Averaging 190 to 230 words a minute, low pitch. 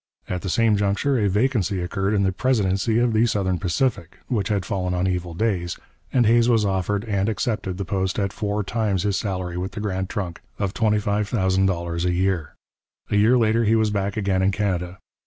Yes: average, 195 wpm; low, 100 Hz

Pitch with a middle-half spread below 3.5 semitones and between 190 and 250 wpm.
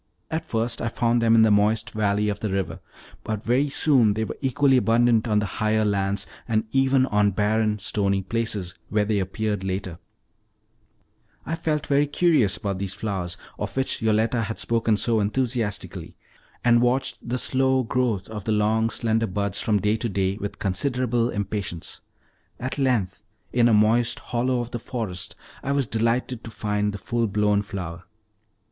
No: average, 2.8 semitones; average, 170 wpm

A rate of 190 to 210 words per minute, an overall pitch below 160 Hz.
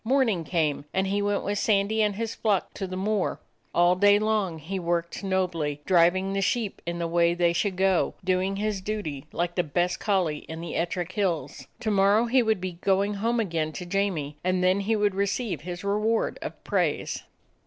No: average, 195 wpm; high, 190 Hz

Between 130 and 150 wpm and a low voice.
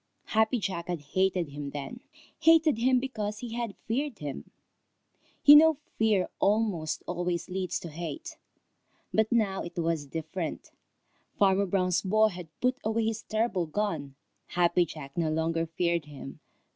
No: average, 145 wpm; medium, 185 Hz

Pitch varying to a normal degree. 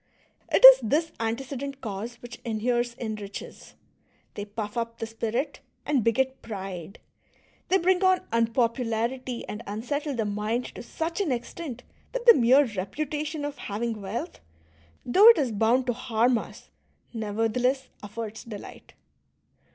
Yes: average, 4.0 semitones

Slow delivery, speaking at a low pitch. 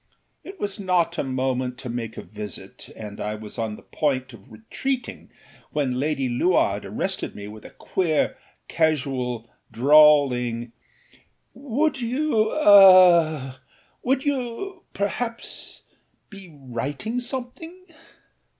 No: slow, 110 wpm; medium, 155 Hz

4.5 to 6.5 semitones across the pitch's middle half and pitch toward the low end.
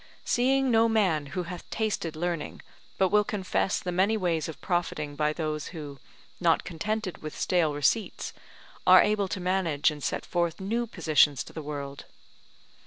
No: average, 5.0 semitones; medium, 175 Hz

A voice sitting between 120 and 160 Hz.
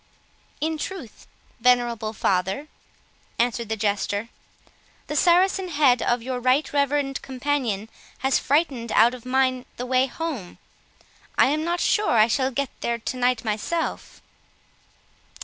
No: very high, 255 Hz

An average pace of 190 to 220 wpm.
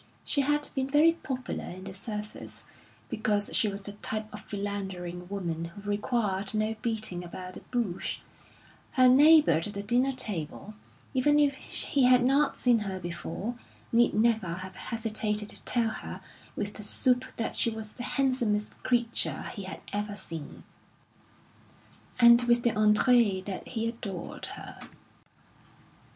No: average, 150 wpm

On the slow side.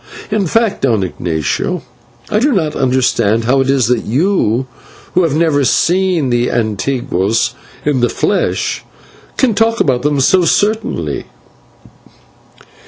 Yes: slow, 130 wpm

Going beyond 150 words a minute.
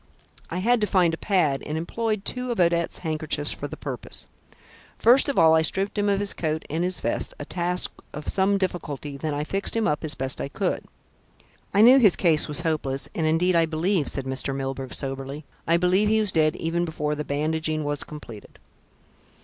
Yes: fast, 205 wpm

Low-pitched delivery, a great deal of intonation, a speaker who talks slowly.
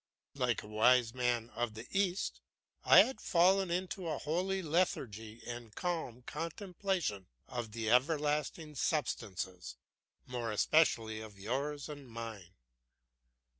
Yes: low, 125 Hz; wide, 6.7 semitones; slow, 120 wpm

